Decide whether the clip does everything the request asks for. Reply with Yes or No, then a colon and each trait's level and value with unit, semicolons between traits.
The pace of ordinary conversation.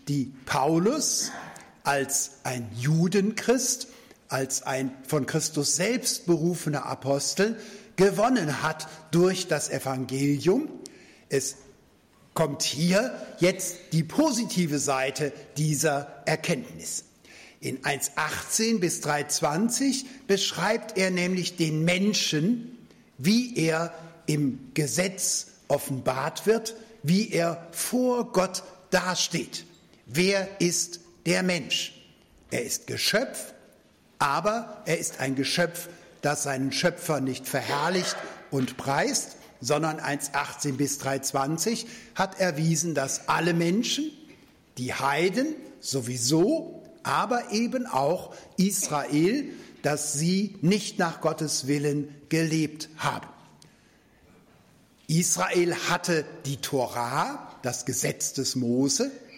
No: slow, 100 wpm